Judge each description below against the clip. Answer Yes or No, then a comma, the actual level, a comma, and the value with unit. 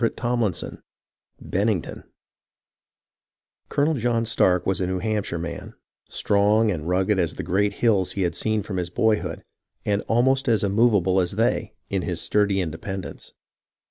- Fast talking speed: No, average, 145 wpm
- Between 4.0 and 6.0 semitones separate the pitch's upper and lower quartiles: No, average, 3.5 semitones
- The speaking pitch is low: Yes, low, 100 Hz